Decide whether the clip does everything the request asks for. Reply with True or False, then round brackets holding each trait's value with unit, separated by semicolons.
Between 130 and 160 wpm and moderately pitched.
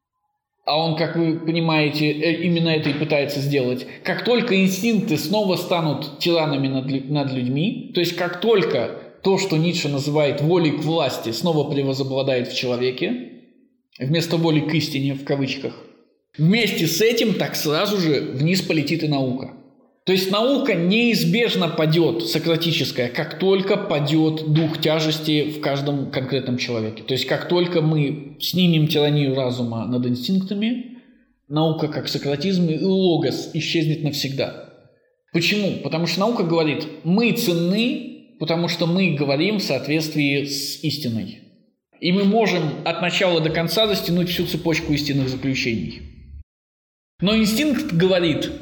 True (140 wpm; 160 Hz)